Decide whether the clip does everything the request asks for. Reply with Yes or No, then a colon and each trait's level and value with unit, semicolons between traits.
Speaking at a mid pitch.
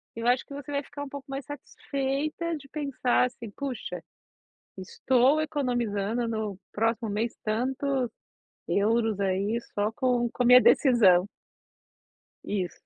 No: high, 245 Hz